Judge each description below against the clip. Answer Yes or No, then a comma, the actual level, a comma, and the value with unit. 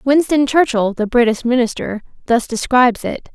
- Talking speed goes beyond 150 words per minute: No, average, 145 wpm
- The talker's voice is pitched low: No, high, 245 Hz